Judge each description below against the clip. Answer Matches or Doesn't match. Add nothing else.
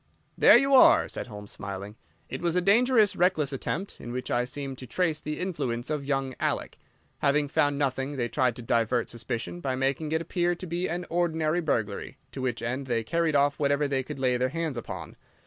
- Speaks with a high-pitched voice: Doesn't match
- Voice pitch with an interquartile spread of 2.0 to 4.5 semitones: Doesn't match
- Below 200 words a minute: Doesn't match